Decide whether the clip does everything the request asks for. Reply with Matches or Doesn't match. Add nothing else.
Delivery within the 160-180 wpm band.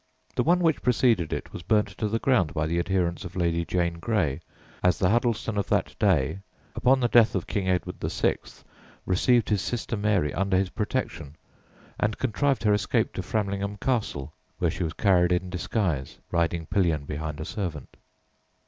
Matches